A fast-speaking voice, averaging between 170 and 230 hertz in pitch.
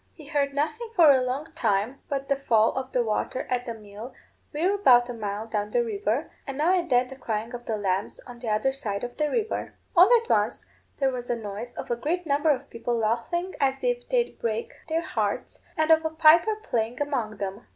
No: fast, 225 wpm; very high, 255 Hz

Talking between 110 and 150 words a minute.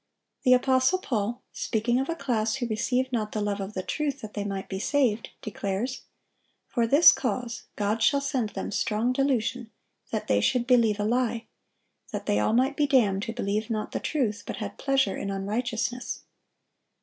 No: average, 185 wpm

